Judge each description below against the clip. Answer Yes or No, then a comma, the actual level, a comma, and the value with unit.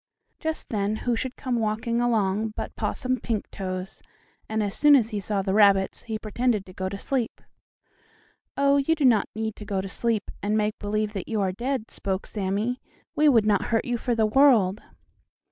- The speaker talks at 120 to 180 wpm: No, average, 195 wpm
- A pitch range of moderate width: Yes, average, 3.2 semitones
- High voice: Yes, high, 215 Hz